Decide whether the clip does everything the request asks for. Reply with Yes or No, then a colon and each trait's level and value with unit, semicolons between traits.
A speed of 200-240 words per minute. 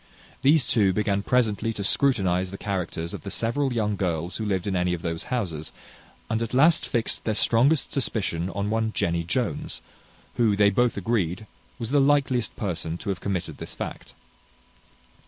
No: average, 175 wpm